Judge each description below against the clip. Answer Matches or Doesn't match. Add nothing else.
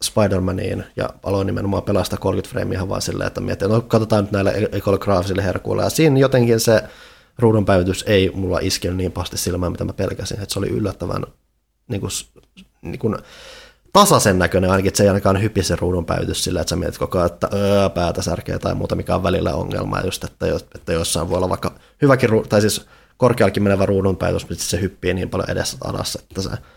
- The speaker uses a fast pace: Matches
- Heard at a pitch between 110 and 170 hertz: Doesn't match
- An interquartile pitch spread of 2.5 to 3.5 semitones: Matches